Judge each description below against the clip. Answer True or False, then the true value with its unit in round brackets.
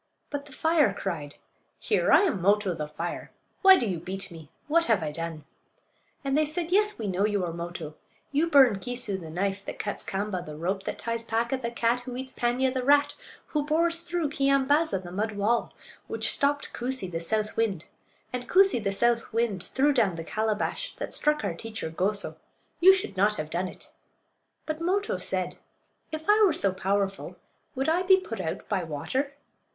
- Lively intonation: True (7.4 semitones)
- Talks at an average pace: True (195 wpm)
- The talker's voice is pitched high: True (230 Hz)